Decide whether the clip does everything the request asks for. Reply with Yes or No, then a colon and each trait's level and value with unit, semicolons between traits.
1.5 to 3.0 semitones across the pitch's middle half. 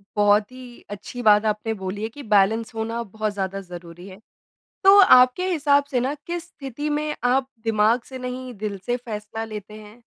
No: average, 3.5 semitones